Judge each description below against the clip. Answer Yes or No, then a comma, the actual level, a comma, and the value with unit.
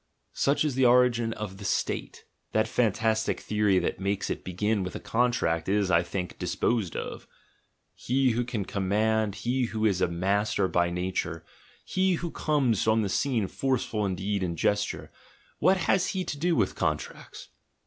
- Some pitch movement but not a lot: Yes, average, 4.4 semitones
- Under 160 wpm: No, average, 180 wpm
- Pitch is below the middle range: Yes, low, 110 Hz